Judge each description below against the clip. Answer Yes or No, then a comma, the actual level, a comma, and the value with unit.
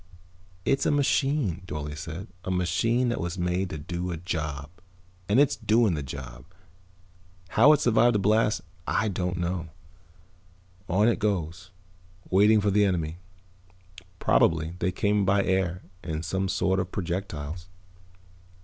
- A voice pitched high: No, very low, 95 Hz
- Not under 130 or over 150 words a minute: Yes, average, 140 wpm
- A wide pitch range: No, average, 3.8 semitones